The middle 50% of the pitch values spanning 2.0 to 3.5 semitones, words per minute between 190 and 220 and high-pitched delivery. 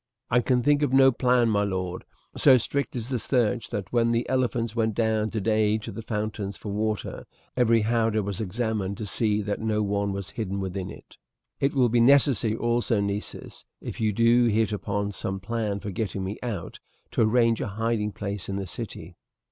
No: narrow, 2.6 semitones; average, 195 wpm; low, 110 Hz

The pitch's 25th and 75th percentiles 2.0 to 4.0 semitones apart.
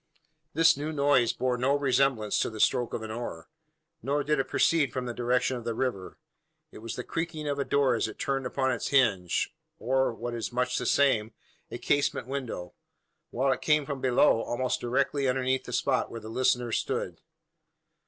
Yes: average, 2.9 semitones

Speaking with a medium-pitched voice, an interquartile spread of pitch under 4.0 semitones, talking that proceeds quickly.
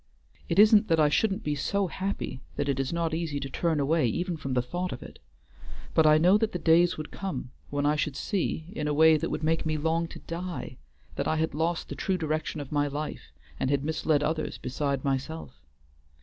Yes: medium, 155 Hz; average, 2.8 semitones; fast, 220 wpm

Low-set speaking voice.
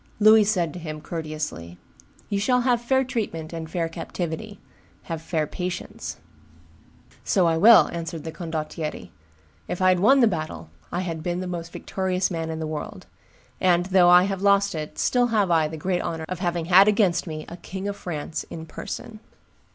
No: medium, 175 Hz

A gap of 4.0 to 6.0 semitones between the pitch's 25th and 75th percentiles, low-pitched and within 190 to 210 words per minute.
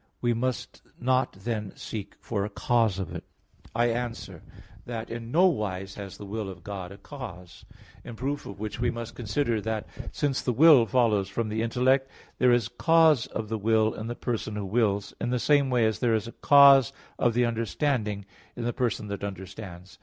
No: average, 3.3 semitones; low, 115 Hz; average, 200 wpm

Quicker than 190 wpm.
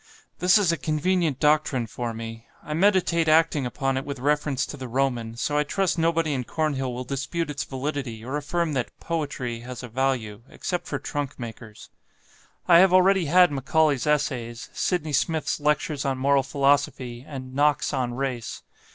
No: average, 170 wpm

